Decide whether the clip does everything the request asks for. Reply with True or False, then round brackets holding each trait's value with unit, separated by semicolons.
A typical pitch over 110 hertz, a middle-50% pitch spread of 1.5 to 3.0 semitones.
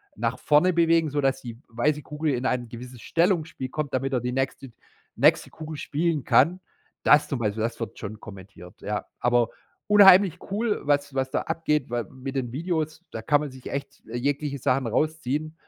False (140 Hz; 4.3 semitones)